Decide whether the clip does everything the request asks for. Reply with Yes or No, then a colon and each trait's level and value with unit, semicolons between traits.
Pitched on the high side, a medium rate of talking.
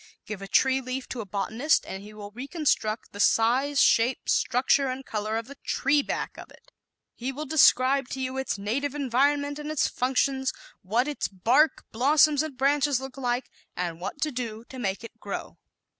Yes: very high, 260 Hz; average, 190 wpm